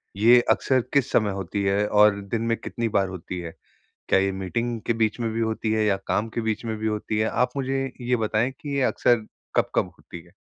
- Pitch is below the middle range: Yes, low, 110 Hz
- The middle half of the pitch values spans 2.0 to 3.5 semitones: Yes, average, 2.7 semitones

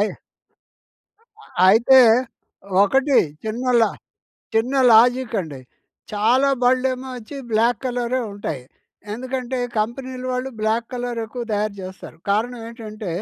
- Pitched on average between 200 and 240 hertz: Yes, high, 235 Hz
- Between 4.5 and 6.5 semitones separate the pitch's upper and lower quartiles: No, average, 3.0 semitones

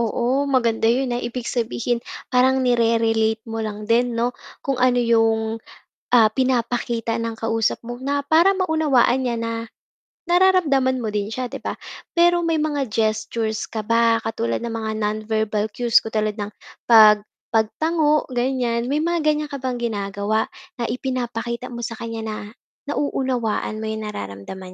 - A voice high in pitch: Yes, high, 235 Hz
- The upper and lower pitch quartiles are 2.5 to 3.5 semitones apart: Yes, average, 2.8 semitones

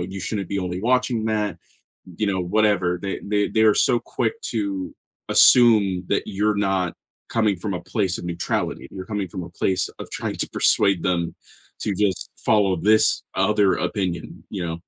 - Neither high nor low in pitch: No, low, 100 Hz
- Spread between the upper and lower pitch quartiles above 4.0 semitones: No, average, 2.7 semitones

